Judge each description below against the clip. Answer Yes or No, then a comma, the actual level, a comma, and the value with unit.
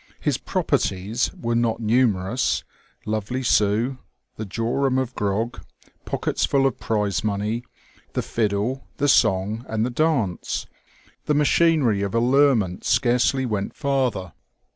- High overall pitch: No, low, 115 Hz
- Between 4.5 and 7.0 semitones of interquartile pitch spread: No, average, 4.0 semitones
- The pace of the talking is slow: Yes, slow, 125 wpm